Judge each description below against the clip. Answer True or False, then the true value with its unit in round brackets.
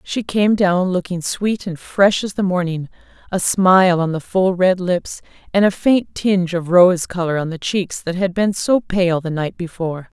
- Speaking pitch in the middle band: True (180 Hz)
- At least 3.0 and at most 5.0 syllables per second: True (4.5 syllables/s)